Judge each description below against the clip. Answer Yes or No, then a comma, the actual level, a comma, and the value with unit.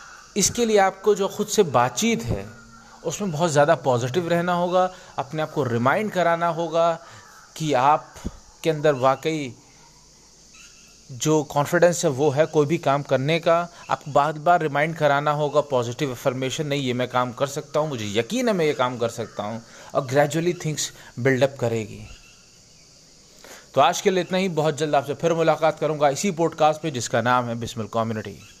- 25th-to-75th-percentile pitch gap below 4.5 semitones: No, average, 5.0 semitones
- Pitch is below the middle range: No, medium, 150 Hz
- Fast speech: No, average, 175 wpm